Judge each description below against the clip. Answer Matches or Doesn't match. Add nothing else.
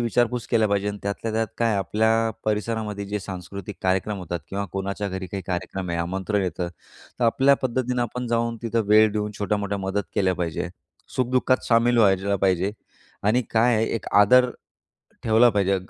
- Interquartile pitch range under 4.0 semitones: Matches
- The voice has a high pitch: Doesn't match